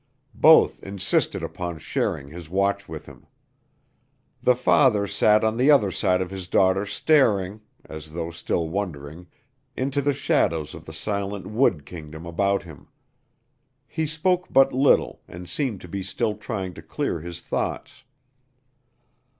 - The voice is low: Yes, very low, 95 Hz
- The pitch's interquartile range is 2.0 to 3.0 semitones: No, average, 4.4 semitones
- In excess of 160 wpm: No, average, 145 wpm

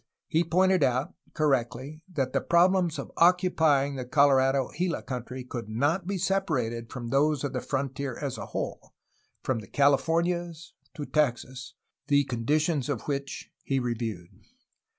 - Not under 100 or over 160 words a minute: Yes, average, 150 wpm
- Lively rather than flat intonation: No, average, 4.5 semitones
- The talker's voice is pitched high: No, medium, 140 Hz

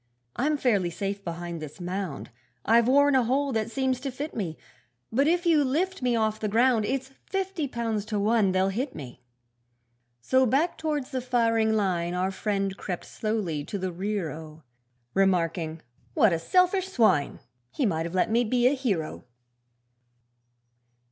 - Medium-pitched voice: No, high, 220 Hz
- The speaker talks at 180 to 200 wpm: No, average, 165 wpm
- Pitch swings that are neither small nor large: No, wide, 6.1 semitones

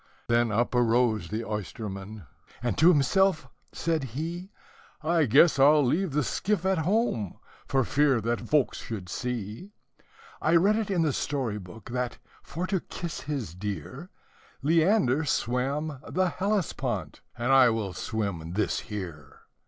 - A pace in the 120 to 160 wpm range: Yes, average, 145 wpm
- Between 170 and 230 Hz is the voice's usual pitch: No, low, 130 Hz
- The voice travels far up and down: Yes, wide, 7.0 semitones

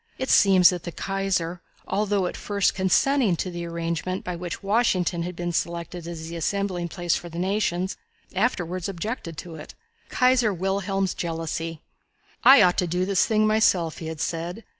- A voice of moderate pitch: Yes, medium, 180 Hz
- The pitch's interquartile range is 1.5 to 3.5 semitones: Yes, average, 2.7 semitones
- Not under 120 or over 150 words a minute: No, average, 170 wpm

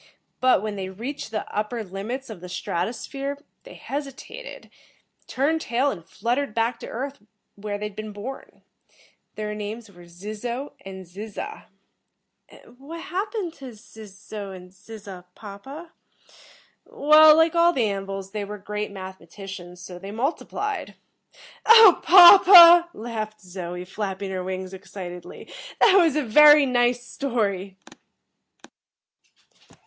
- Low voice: No, high, 215 Hz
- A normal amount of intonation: No, wide, 6.3 semitones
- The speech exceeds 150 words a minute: No, slow, 135 wpm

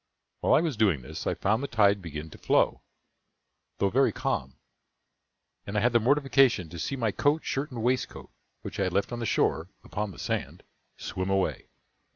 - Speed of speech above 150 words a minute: Yes, average, 195 wpm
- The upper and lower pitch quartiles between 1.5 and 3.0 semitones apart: No, wide, 5.5 semitones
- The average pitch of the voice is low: Yes, low, 105 Hz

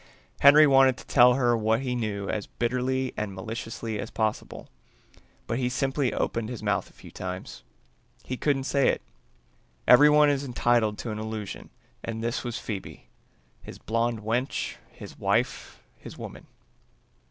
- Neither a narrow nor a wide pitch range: Yes, average, 3.1 semitones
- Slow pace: No, average, 155 wpm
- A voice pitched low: Yes, low, 120 Hz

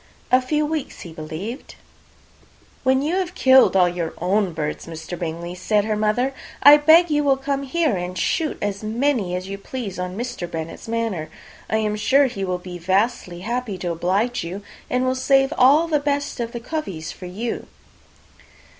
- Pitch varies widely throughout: Yes, wide, 6.9 semitones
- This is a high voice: Yes, high, 220 Hz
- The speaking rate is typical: Yes, average, 180 wpm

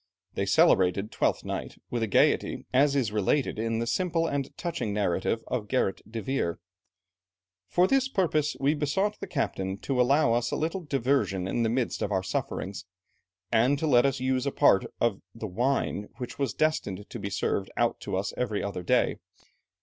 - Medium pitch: No, low, 120 Hz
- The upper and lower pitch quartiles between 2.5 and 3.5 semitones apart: No, wide, 5.6 semitones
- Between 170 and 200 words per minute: Yes, average, 180 wpm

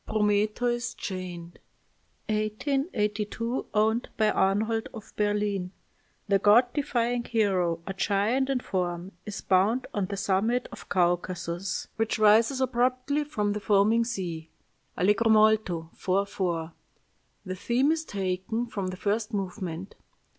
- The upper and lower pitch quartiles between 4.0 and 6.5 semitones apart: No, average, 3.6 semitones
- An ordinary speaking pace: No, slow, 125 wpm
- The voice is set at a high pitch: Yes, high, 210 Hz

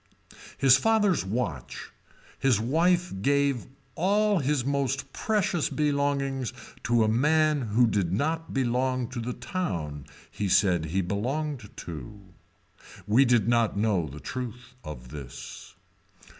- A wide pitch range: Yes, wide, 6.1 semitones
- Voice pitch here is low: Yes, low, 125 Hz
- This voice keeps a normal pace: No, slow, 125 wpm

